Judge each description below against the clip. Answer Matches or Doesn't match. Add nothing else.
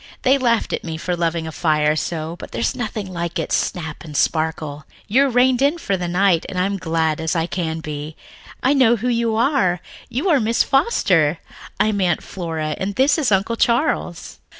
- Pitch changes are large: Matches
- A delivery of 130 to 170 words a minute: Doesn't match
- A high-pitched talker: Doesn't match